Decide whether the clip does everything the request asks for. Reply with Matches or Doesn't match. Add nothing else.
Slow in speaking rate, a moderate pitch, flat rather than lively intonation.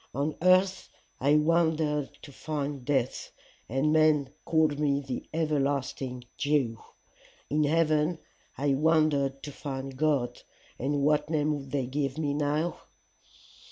Matches